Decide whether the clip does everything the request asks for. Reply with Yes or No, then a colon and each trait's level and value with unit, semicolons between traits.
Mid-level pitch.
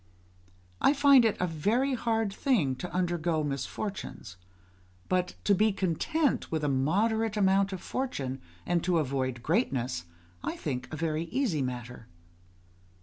Yes: medium, 175 Hz